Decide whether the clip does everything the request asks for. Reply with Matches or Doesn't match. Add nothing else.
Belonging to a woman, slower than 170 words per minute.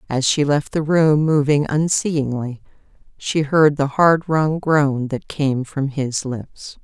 Matches